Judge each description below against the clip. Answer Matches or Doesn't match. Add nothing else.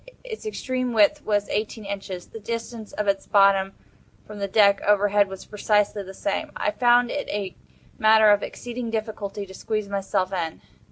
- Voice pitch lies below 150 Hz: Doesn't match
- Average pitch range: Doesn't match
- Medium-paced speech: Matches